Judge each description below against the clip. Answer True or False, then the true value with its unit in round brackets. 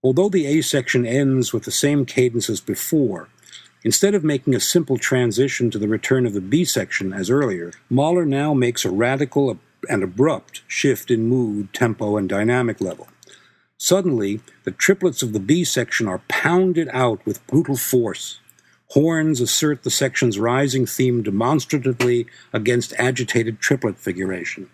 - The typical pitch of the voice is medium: False (125 Hz)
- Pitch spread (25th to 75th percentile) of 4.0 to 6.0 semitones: False (3.5 semitones)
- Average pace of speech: True (155 wpm)